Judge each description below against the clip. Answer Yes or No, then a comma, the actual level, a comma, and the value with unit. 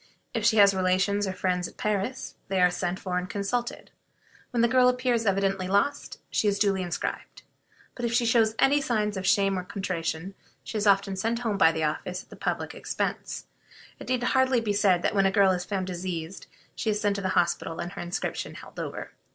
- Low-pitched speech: No, high, 195 Hz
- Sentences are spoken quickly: Yes, fast, 210 wpm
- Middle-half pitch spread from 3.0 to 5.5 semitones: Yes, average, 3.3 semitones